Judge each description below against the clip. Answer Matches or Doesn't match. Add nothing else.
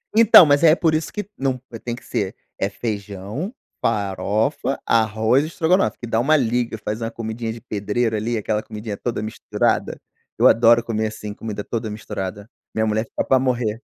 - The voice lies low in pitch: Matches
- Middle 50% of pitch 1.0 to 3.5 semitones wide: Matches